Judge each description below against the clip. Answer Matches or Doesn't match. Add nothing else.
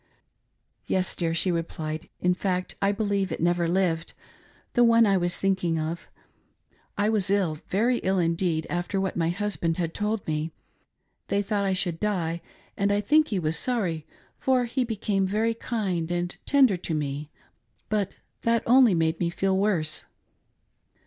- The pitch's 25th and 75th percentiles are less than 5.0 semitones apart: Matches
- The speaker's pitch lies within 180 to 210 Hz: Matches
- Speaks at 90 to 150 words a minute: Doesn't match